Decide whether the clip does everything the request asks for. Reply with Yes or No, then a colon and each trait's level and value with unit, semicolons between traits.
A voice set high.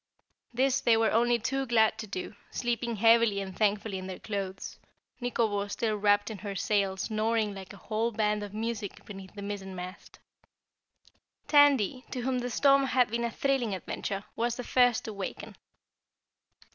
Yes: high, 220 Hz